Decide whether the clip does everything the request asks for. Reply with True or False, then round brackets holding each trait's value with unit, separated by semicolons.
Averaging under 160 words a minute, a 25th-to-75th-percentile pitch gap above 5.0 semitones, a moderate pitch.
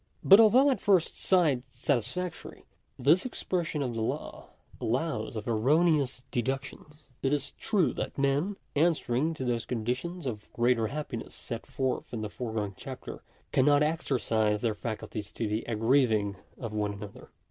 False (150 wpm; 5.6 semitones; 130 Hz)